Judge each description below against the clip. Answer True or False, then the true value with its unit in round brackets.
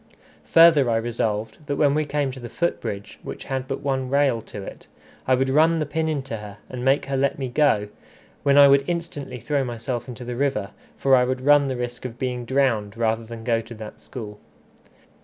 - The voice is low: True (130 Hz)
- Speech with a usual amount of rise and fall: True (3.4 semitones)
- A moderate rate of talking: False (215 wpm)